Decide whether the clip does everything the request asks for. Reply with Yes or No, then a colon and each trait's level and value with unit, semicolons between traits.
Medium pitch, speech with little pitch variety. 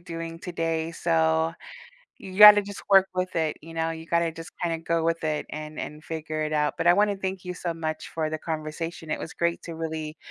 Yes: medium, 165 Hz; narrow, 1.5 semitones